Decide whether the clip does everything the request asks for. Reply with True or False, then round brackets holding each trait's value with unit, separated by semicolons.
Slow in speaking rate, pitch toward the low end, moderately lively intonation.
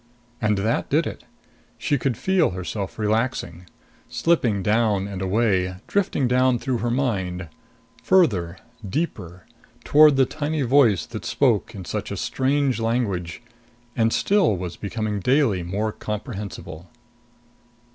False (125 wpm; 110 Hz; 5.8 semitones)